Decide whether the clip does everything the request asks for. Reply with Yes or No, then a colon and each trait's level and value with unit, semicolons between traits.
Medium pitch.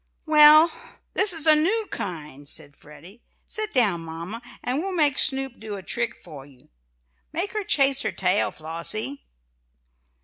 No: high, 245 Hz